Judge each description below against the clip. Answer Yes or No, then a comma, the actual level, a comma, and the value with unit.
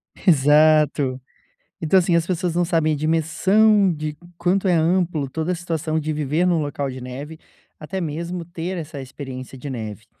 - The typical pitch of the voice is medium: Yes, medium, 160 Hz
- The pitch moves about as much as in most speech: Yes, average, 3.3 semitones